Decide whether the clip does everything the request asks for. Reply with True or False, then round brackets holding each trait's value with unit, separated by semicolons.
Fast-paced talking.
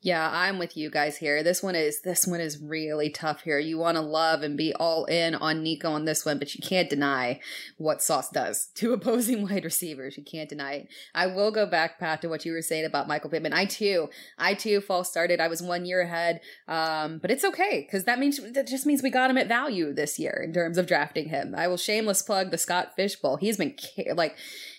True (240 wpm)